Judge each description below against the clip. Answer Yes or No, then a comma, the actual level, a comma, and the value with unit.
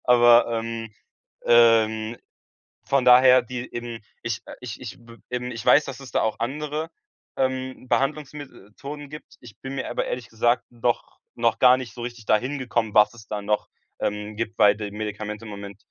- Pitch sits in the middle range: No, low, 120 Hz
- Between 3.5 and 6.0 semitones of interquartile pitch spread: No, average, 2.9 semitones